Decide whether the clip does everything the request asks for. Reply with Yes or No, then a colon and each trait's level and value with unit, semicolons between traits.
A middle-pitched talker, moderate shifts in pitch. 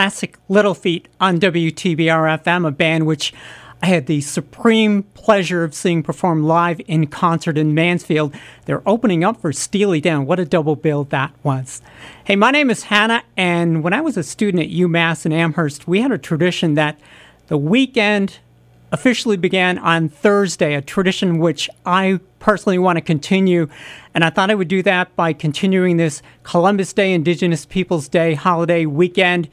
Yes: medium, 175 Hz; average, 3.3 semitones